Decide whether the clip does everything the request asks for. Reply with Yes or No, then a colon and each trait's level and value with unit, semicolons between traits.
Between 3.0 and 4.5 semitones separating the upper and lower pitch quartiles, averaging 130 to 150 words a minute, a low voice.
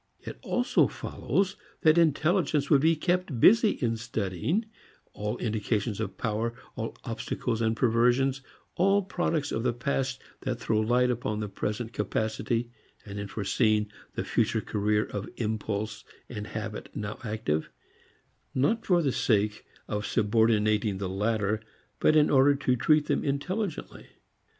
No: average, 5.1 semitones; average, 140 wpm; low, 115 Hz